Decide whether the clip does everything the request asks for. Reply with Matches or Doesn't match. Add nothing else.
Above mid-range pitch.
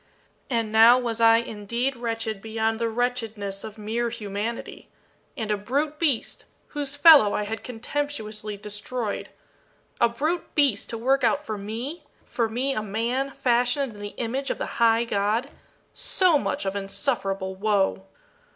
Matches